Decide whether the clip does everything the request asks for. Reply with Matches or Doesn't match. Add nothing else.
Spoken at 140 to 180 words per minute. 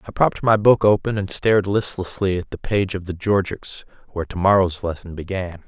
Doesn't match